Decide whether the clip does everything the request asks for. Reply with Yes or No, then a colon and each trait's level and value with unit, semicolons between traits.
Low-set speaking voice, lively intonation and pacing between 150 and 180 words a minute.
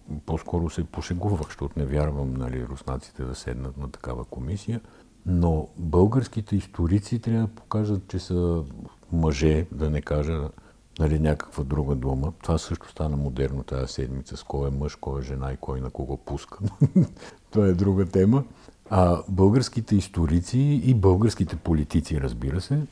Yes: very low, 80 Hz; wide, 5.8 semitones; average, 155 wpm